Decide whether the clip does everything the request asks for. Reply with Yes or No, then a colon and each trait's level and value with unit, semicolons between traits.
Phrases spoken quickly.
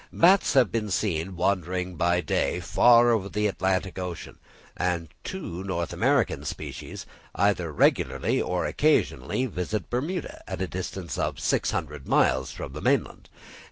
No: average, 140 wpm